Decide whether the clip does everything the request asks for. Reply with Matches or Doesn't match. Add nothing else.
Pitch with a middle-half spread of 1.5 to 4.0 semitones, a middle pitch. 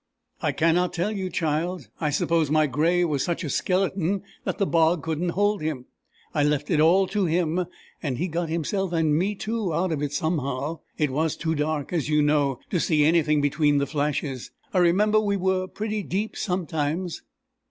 Matches